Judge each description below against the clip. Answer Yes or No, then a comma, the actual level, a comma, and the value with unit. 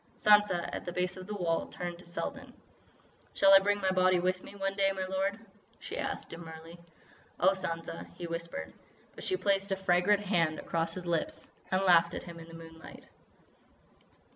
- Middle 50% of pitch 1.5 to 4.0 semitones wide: Yes, narrow, 2.5 semitones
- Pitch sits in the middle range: Yes, medium, 180 Hz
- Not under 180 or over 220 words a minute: Yes, average, 185 wpm